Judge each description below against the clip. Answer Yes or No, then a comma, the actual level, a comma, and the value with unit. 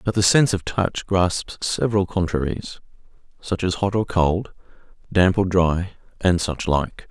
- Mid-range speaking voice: No, very low, 95 Hz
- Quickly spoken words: No, average, 150 wpm